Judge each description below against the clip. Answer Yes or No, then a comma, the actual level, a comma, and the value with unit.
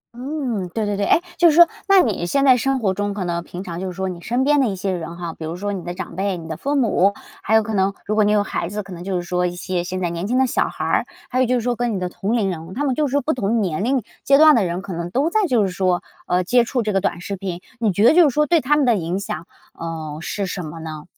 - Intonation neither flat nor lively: No, wide, 5.8 semitones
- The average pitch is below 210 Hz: Yes, high, 200 Hz